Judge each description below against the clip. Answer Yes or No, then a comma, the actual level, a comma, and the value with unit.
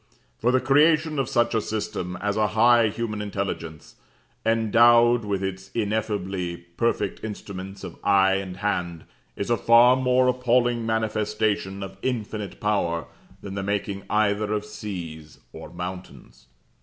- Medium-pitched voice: No, low, 105 Hz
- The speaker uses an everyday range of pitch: Yes, average, 3.4 semitones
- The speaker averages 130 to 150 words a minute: Yes, average, 140 wpm